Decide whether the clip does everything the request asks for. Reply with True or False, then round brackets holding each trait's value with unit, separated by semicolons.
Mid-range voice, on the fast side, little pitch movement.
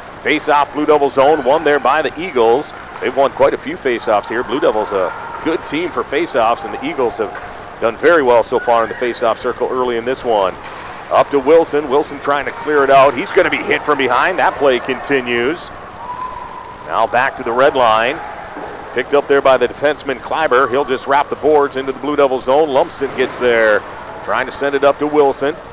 True (145 Hz; 225 wpm; 1.9 semitones)